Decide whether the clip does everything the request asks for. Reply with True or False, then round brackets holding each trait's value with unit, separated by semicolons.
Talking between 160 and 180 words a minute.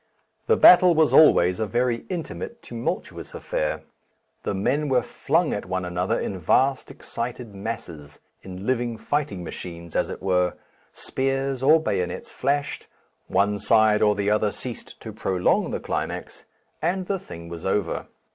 False (150 wpm)